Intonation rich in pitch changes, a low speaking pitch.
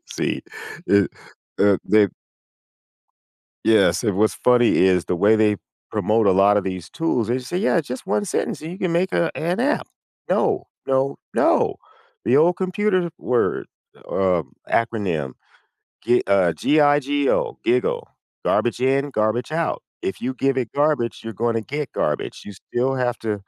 Yes: wide, 6.9 semitones; low, 125 Hz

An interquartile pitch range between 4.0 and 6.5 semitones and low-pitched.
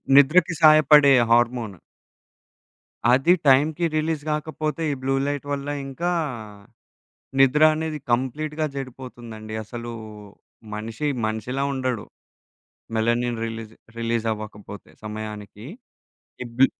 Yes: average, 4.8 semitones; low, 130 Hz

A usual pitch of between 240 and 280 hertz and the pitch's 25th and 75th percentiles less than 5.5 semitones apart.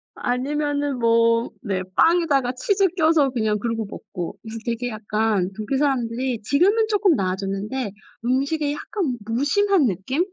Yes: very high, 250 Hz; average, 5.1 semitones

